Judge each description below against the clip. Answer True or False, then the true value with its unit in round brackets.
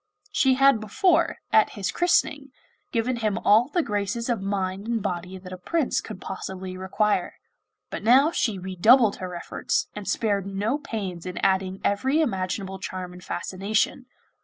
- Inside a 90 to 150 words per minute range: False (160 wpm)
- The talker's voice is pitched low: False (205 Hz)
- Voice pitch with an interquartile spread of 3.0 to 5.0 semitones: True (4.0 semitones)